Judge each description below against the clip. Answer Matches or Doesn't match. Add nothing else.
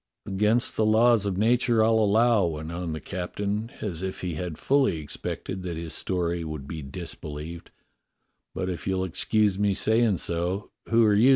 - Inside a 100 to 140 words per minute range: Doesn't match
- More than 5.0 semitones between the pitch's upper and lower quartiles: Doesn't match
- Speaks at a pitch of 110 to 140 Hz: Doesn't match